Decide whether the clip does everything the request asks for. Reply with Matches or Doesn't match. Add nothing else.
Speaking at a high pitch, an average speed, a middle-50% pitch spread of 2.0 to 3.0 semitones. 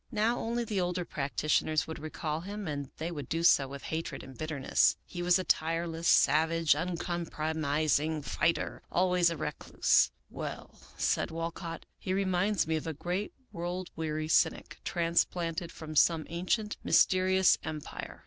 Doesn't match